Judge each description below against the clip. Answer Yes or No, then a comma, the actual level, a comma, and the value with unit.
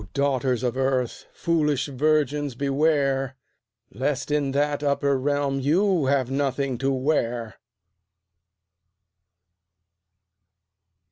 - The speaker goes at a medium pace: No, slow, 85 wpm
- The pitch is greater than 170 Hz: No, medium, 140 Hz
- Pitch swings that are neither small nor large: No, narrow, 1.8 semitones